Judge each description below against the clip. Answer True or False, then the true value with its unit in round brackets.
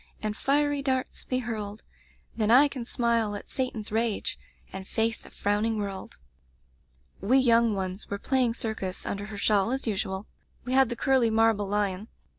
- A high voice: True (225 Hz)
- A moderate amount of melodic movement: True (3.5 semitones)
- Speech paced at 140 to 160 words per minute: False (170 wpm)